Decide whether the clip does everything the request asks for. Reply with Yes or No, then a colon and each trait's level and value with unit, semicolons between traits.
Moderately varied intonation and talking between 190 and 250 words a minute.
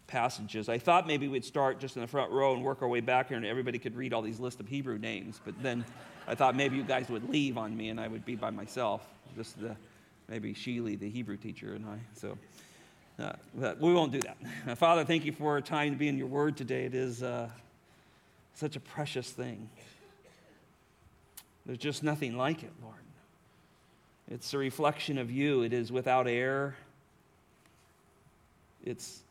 Yes: average, 3.3 semitones; average, 195 wpm